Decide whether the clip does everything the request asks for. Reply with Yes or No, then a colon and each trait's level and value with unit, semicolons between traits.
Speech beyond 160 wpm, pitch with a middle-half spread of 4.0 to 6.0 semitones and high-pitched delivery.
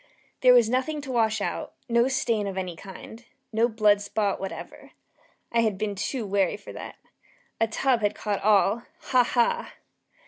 No: average, 170 wpm; average, 3.1 semitones; high, 220 Hz